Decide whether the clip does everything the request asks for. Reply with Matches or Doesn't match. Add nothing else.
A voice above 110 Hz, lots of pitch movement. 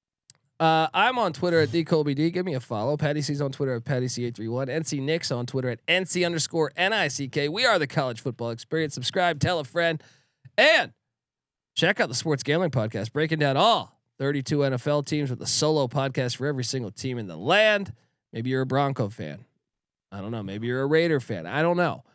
Doesn't match